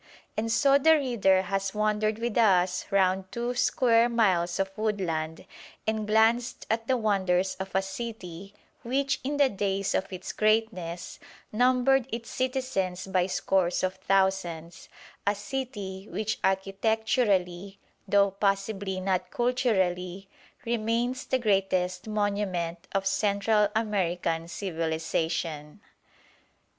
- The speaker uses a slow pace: Yes, slow, 115 wpm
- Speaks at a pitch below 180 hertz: No, high, 200 Hz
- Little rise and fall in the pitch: No, average, 3.3 semitones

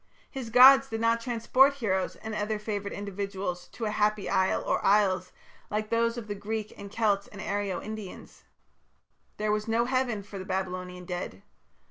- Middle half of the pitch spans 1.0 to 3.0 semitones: Yes, average, 2.7 semitones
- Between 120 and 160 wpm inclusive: No, average, 170 wpm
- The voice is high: Yes, high, 210 Hz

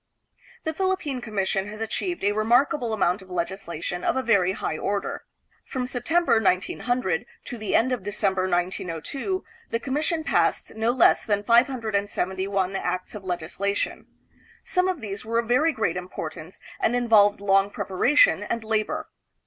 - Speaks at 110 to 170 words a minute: Yes, average, 155 wpm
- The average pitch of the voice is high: Yes, high, 215 Hz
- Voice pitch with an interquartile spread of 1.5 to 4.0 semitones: No, average, 4.6 semitones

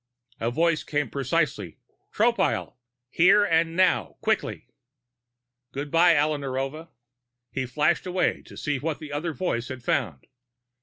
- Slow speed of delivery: Yes, slow, 125 wpm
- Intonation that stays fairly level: No, average, 3.8 semitones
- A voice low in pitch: No, medium, 150 Hz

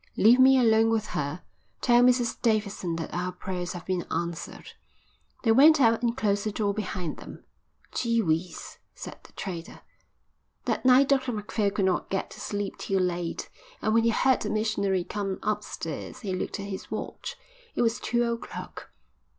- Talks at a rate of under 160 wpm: No, average, 175 wpm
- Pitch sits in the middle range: No, high, 210 Hz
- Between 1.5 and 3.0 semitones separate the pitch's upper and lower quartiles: No, average, 4.1 semitones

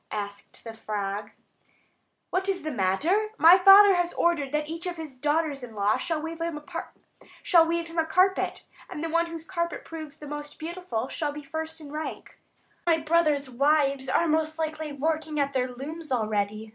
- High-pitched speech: Yes, very high, 310 Hz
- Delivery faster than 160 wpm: Yes, average, 170 wpm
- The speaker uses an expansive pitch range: No, average, 3.5 semitones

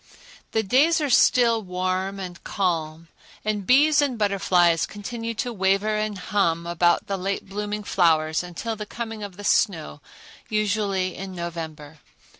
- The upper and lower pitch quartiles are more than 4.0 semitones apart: No, average, 3.6 semitones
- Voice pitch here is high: Yes, high, 195 Hz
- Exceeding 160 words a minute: No, average, 145 wpm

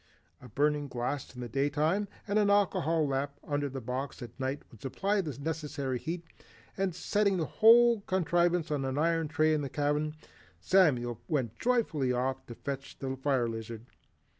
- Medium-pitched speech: Yes, medium, 145 Hz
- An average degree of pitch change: Yes, average, 4.5 semitones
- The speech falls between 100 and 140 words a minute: No, average, 175 wpm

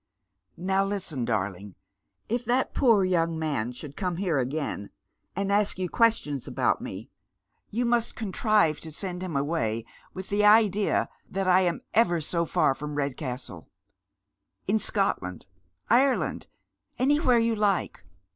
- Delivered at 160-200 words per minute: No, average, 145 wpm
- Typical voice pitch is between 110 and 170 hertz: No, medium, 185 Hz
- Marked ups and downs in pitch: Yes, wide, 6.2 semitones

